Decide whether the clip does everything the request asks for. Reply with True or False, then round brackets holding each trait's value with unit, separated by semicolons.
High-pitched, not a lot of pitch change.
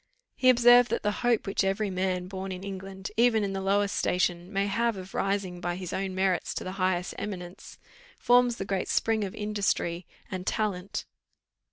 True (195 Hz; 2.3 semitones)